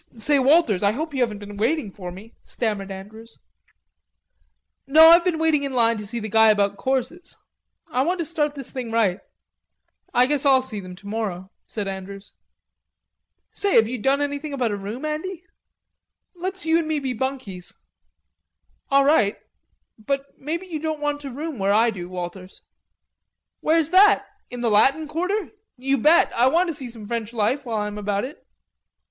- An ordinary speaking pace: Yes, average, 180 wpm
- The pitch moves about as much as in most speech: No, wide, 6.5 semitones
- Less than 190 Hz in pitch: No, very high, 255 Hz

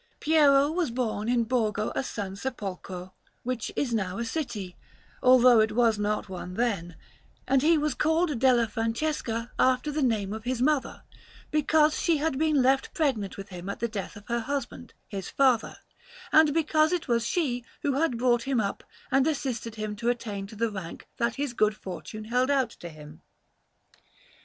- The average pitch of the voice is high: Yes, high, 240 Hz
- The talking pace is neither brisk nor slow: Yes, average, 180 wpm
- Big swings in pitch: No, average, 4.5 semitones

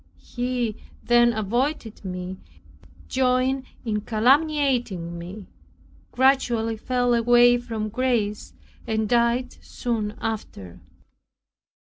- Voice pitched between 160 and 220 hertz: No, high, 235 Hz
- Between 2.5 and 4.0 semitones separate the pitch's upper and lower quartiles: Yes, average, 2.8 semitones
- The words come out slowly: Yes, slow, 85 wpm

